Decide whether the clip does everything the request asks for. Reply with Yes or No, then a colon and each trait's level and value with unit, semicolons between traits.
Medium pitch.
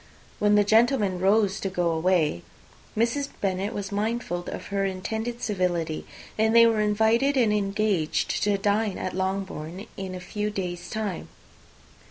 No: high, 200 Hz